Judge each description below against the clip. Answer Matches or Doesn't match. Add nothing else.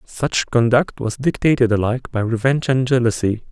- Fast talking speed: Doesn't match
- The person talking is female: Doesn't match